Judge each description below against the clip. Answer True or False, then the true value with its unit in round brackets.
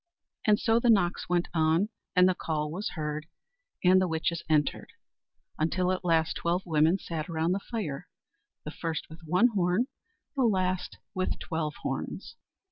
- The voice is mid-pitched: True (175 Hz)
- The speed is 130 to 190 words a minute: True (160 wpm)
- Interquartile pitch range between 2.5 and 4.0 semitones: True (2.8 semitones)